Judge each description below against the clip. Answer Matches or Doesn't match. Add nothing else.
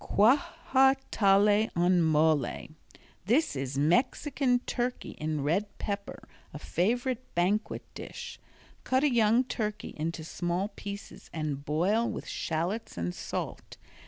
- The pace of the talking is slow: Matches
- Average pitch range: Doesn't match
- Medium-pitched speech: Doesn't match